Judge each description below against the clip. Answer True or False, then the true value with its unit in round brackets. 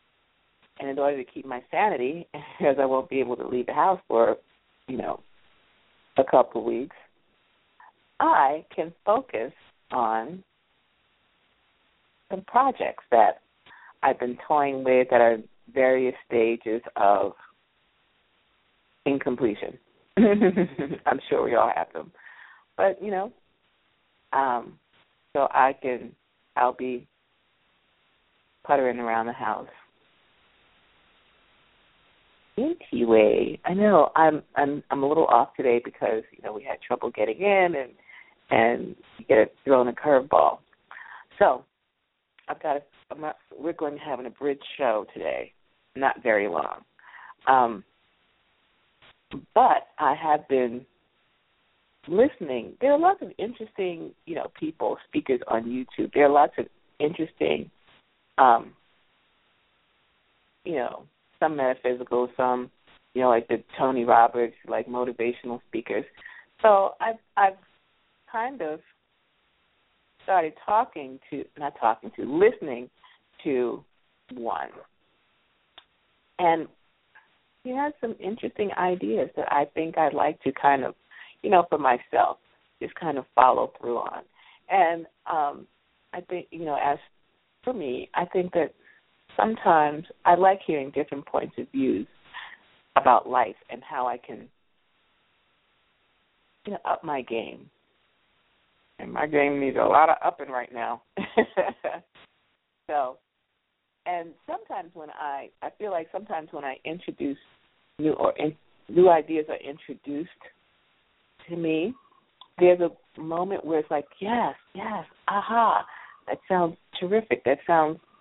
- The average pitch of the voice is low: False (150 Hz)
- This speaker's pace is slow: True (130 wpm)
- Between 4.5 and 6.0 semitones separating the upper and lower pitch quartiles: False (6.5 semitones)